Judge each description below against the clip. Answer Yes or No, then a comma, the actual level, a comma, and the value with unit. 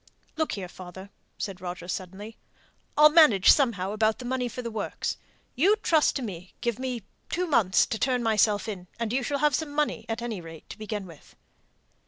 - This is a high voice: Yes, high, 225 Hz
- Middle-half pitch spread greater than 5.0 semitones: Yes, wide, 5.5 semitones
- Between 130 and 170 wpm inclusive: No, average, 195 wpm